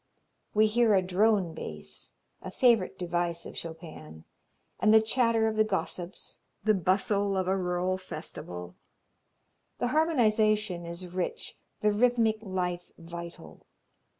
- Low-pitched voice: No, high, 190 Hz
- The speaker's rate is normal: No, slow, 125 wpm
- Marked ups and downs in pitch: No, average, 3.9 semitones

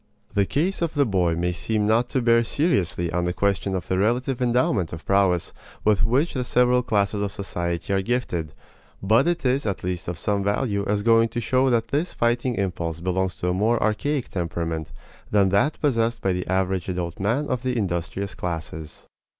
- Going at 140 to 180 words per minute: No, average, 195 wpm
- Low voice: Yes, low, 100 Hz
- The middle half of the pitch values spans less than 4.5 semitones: No, average, 5.3 semitones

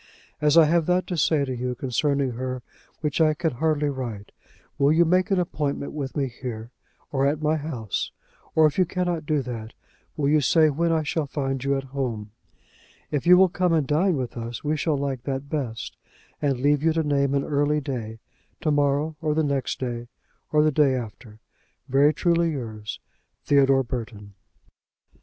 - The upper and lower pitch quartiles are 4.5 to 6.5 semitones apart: No, average, 3.3 semitones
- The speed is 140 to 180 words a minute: No, average, 190 wpm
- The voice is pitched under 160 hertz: Yes, medium, 140 Hz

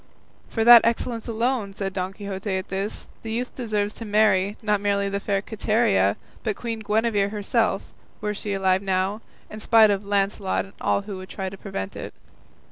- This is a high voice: Yes, high, 205 Hz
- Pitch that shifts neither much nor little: No, narrow, 2.1 semitones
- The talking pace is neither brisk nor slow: Yes, average, 185 wpm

